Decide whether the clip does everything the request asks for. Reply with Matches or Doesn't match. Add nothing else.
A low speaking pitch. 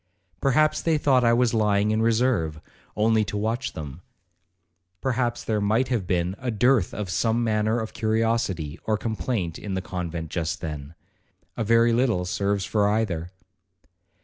Matches